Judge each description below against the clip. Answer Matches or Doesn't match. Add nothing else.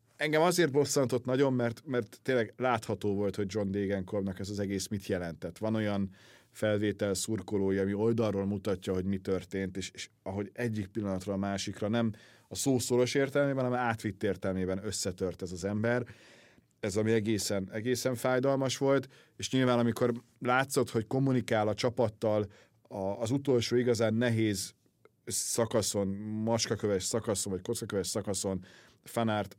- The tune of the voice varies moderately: Matches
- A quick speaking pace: Doesn't match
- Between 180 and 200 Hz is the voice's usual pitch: Doesn't match